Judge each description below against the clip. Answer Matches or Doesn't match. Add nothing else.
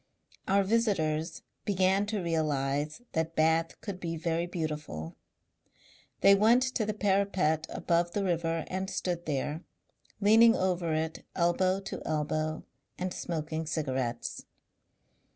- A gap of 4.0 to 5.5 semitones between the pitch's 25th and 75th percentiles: Doesn't match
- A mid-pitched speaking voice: Matches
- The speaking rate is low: Matches